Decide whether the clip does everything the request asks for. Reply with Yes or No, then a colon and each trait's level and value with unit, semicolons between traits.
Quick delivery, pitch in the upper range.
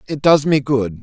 No: fast, 235 wpm; low, 135 Hz